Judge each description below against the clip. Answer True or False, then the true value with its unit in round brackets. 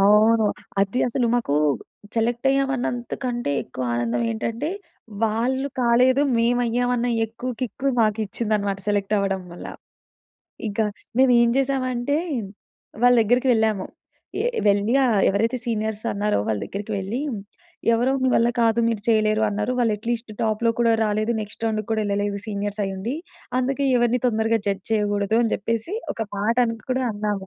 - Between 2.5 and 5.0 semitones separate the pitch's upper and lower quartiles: True (2.9 semitones)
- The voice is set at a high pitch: True (225 Hz)